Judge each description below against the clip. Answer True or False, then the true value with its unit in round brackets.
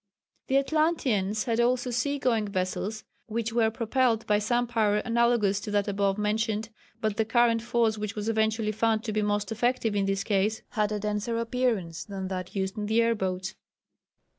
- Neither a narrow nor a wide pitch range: False (2.2 semitones)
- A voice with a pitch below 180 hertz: False (220 Hz)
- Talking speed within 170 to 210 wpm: True (185 wpm)